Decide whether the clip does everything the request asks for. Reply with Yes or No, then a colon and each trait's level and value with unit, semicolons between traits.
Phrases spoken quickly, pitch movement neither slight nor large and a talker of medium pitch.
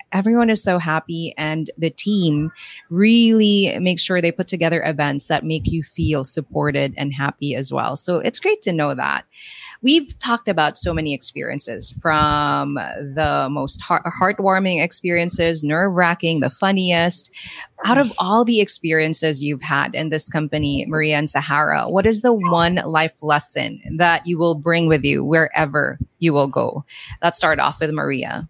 No: average, 165 wpm; average, 3.6 semitones; medium, 165 Hz